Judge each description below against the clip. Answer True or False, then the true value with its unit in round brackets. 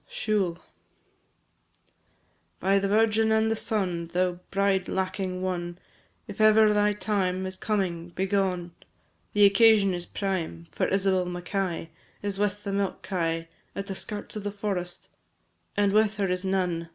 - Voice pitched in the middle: False (195 Hz)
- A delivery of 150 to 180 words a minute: False (140 wpm)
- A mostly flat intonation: True (2.3 semitones)